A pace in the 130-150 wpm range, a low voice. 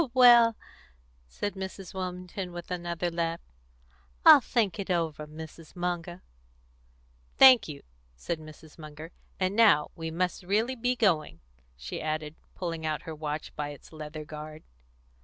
No: average, 140 wpm; medium, 170 Hz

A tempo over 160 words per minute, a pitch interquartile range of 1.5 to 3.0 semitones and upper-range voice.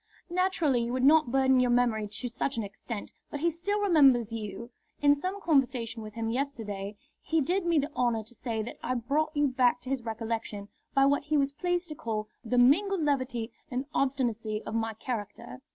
No: average, 200 wpm; average, 4.2 semitones; very high, 255 Hz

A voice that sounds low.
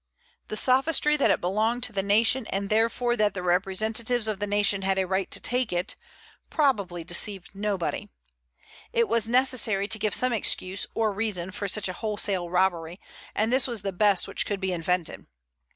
No: high, 205 Hz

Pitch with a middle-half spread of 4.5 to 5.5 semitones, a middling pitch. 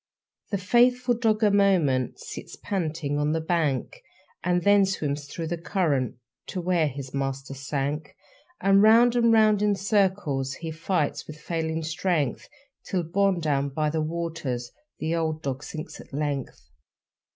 Yes: average, 5.2 semitones; medium, 160 Hz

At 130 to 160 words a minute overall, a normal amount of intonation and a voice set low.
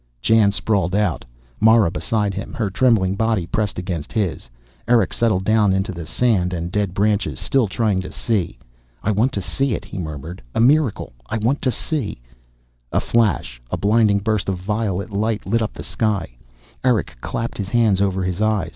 No: average, 185 wpm; average, 3.4 semitones; low, 100 Hz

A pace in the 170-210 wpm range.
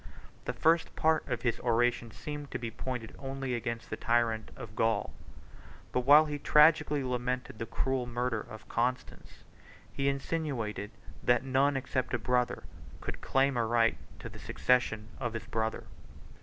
No: average, 155 wpm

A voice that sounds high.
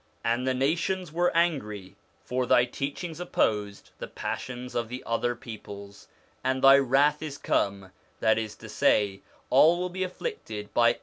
No: low, 125 Hz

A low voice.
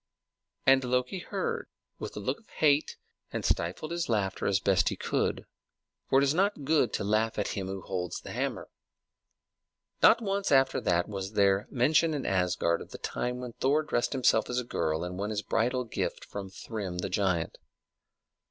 Yes: low, 115 Hz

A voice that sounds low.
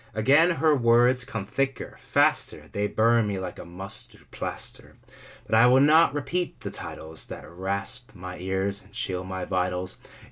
Yes: low, 105 Hz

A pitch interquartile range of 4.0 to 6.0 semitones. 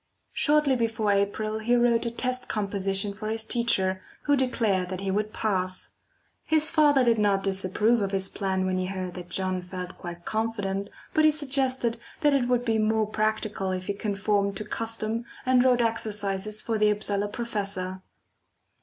No: average, 3.3 semitones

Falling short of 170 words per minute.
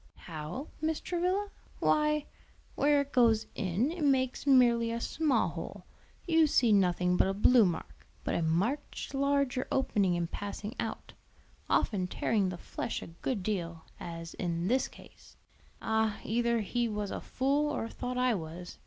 Yes: average, 160 wpm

